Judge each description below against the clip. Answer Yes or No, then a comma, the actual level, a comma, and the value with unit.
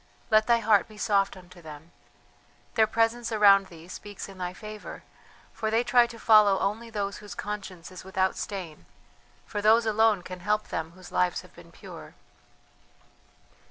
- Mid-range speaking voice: No, high, 205 Hz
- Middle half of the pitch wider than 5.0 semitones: No, average, 3.0 semitones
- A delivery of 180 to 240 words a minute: No, average, 165 wpm